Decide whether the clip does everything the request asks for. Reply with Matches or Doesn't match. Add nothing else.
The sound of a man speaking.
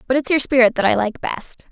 Doesn't match